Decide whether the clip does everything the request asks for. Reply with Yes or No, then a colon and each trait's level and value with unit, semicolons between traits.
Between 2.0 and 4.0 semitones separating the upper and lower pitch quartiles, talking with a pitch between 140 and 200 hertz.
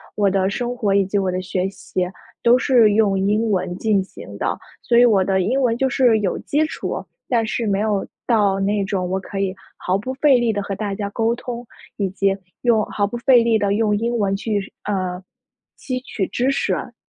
No: average, 3.4 semitones; high, 210 Hz